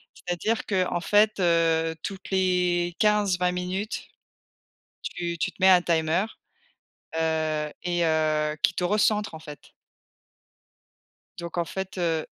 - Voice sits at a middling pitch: Yes, medium, 175 Hz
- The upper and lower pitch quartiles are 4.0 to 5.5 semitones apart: No, average, 2.7 semitones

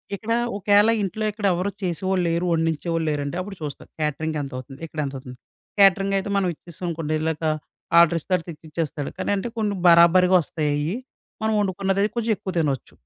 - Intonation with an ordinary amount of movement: Yes, average, 4.1 semitones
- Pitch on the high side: No, medium, 170 Hz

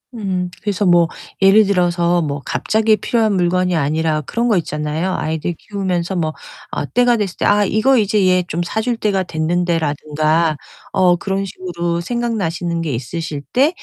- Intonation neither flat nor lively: Yes, average, 3.9 semitones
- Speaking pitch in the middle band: Yes, medium, 180 Hz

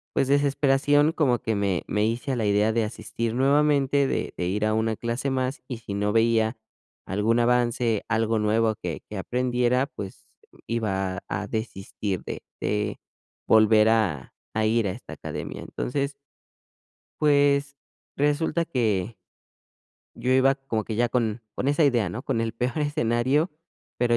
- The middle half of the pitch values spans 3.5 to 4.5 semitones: Yes, average, 4.0 semitones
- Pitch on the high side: No, low, 115 Hz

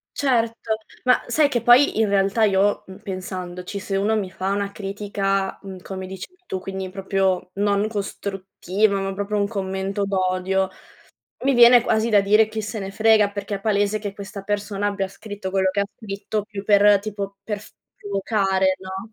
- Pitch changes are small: Yes, narrow, 1.6 semitones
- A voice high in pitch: Yes, high, 200 Hz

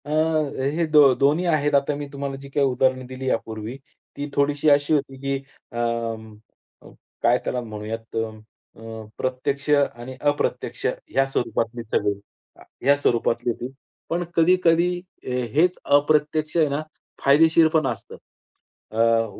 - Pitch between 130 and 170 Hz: Yes, medium, 140 Hz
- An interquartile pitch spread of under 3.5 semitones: No, average, 4.0 semitones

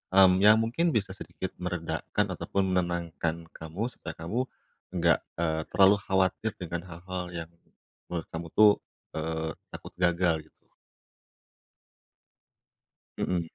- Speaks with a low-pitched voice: Yes, very low, 90 Hz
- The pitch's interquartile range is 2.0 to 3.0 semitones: Yes, narrow, 2.6 semitones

